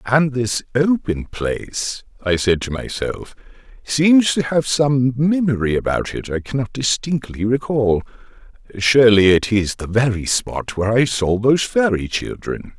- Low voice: Yes, low, 120 Hz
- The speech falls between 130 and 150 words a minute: Yes, average, 140 wpm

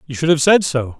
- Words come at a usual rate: No, fast, 300 wpm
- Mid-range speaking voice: Yes, medium, 145 Hz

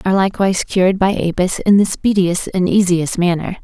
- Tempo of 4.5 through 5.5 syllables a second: No, 5.7 syllables/s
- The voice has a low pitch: No, medium, 185 Hz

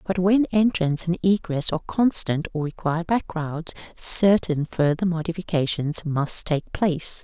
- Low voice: No, medium, 170 Hz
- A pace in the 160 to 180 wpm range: No, average, 140 wpm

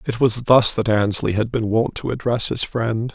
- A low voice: Yes, low, 115 Hz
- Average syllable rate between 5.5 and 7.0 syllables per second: No, 5.0 syllables/s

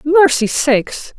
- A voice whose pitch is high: Yes, very high, 290 Hz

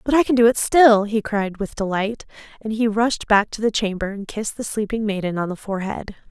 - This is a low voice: No, high, 210 Hz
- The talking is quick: Yes, fast, 240 wpm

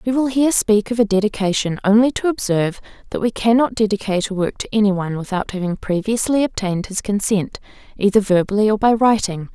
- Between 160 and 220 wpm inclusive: Yes, average, 190 wpm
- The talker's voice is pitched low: No, high, 210 Hz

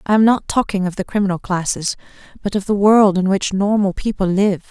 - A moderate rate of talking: No, fast, 215 wpm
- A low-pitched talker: No, high, 195 Hz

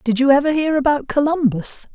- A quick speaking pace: No, average, 185 wpm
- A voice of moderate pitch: No, very high, 280 Hz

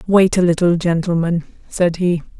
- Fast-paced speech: No, average, 150 wpm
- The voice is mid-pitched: Yes, medium, 175 Hz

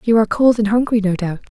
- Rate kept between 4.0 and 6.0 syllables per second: No, 6.8 syllables/s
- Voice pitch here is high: Yes, high, 215 Hz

